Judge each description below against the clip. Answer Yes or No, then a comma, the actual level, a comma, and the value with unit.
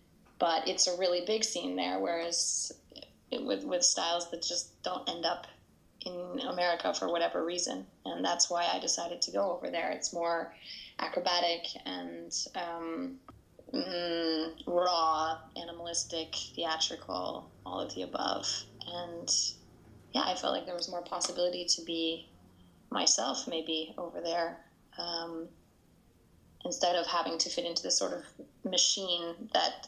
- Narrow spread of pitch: Yes, narrow, 1.4 semitones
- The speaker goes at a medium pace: Yes, average, 145 wpm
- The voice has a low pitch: No, medium, 170 Hz